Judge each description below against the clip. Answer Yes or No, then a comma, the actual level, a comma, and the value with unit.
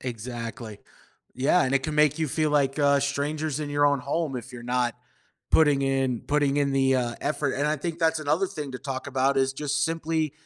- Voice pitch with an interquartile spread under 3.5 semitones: Yes, narrow, 2.4 semitones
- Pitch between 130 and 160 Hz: Yes, medium, 140 Hz